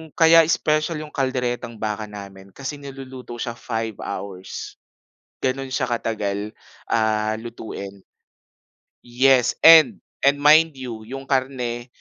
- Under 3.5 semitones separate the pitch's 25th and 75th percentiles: No, average, 3.8 semitones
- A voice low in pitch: Yes, low, 125 Hz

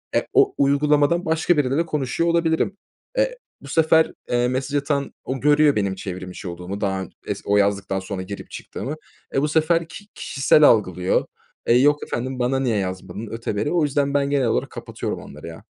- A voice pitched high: No, low, 135 Hz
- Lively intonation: Yes, wide, 6.9 semitones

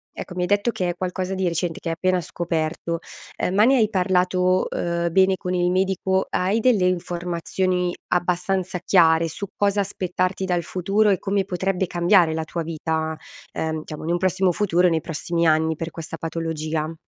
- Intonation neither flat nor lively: No, narrow, 2.3 semitones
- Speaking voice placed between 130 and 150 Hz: No, medium, 180 Hz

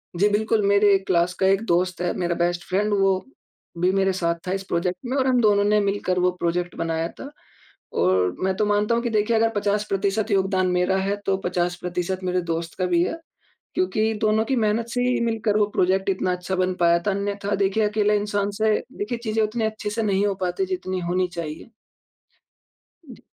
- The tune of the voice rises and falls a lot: No, average, 2.9 semitones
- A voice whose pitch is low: No, high, 195 Hz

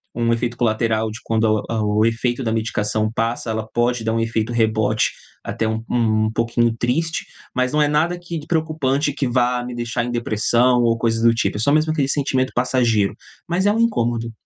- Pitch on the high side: No, low, 120 Hz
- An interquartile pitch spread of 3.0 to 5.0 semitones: No, narrow, 2.6 semitones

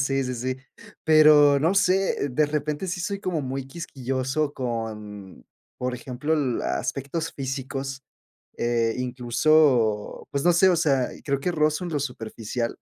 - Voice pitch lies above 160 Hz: No, low, 135 Hz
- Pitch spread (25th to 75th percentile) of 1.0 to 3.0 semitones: No, average, 3.7 semitones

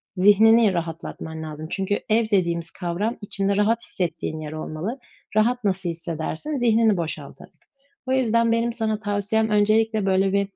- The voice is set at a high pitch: Yes, high, 205 Hz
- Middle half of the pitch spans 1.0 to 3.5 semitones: No, average, 4.5 semitones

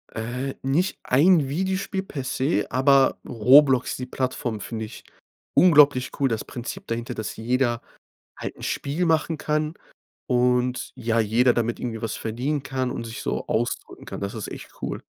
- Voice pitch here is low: Yes, low, 125 Hz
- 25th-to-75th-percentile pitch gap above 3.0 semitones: Yes, average, 3.6 semitones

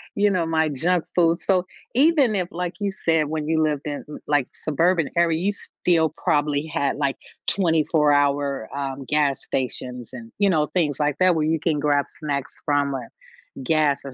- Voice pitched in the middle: Yes, medium, 155 Hz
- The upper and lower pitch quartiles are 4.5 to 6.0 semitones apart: No, average, 3.1 semitones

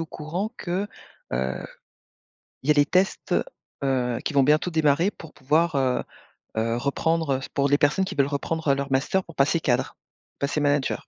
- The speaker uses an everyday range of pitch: Yes, average, 3.2 semitones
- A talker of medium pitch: Yes, medium, 145 Hz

